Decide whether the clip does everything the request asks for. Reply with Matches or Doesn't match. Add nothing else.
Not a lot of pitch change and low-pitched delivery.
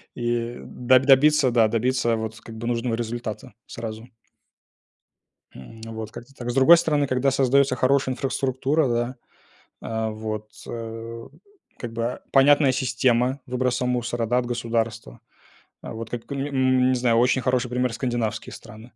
Matches